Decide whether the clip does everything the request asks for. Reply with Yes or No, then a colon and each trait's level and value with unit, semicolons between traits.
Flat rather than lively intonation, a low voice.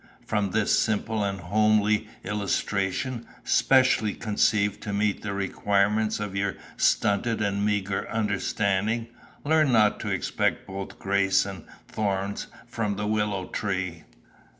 Yes: narrow, 1.6 semitones; low, 105 Hz